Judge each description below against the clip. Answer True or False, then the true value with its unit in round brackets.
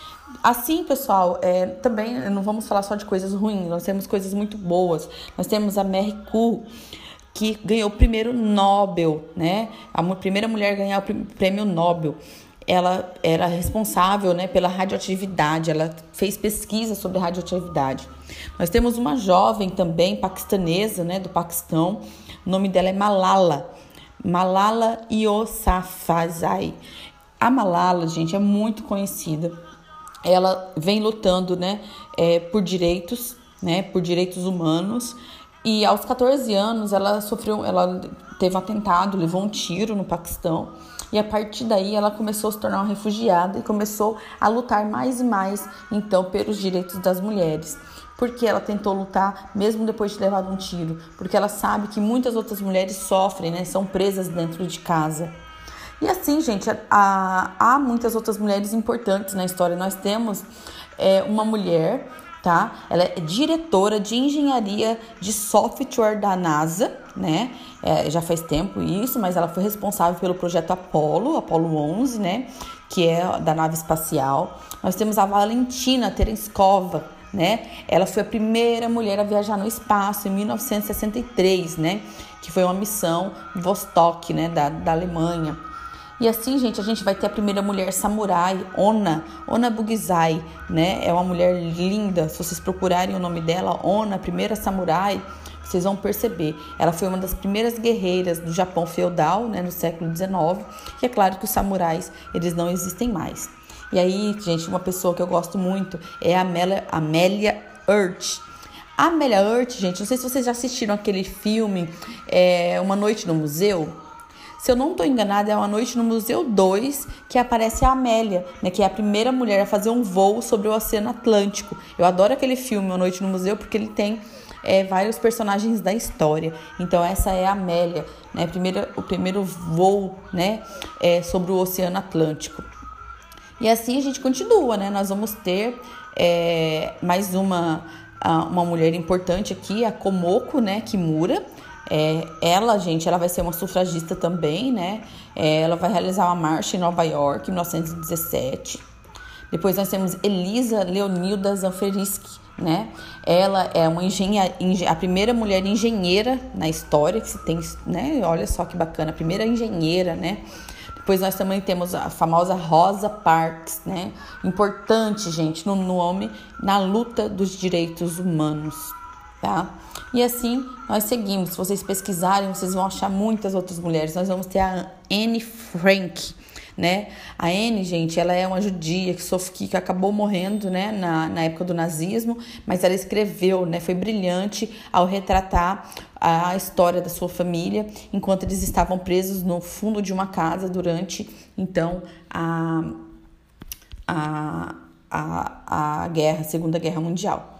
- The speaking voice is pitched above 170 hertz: True (190 Hz)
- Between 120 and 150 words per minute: False (160 wpm)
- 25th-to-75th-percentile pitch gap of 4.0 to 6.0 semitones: False (3.5 semitones)